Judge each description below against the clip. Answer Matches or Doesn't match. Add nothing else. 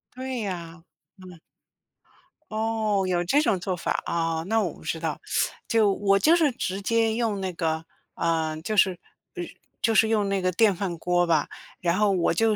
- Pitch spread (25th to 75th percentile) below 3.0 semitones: Doesn't match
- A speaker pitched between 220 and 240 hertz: Doesn't match